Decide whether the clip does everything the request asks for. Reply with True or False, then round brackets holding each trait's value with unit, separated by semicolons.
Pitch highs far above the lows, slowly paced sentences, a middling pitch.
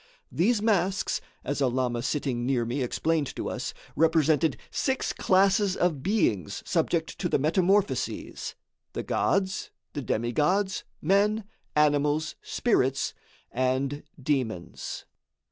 True (6.5 semitones; 110 wpm; 150 Hz)